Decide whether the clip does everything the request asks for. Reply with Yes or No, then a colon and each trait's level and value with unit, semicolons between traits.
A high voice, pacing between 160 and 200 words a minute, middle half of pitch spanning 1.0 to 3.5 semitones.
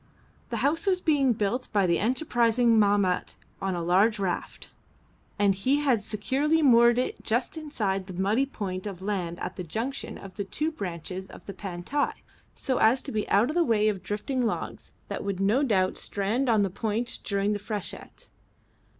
No: high, 210 Hz; average, 185 wpm; average, 4.6 semitones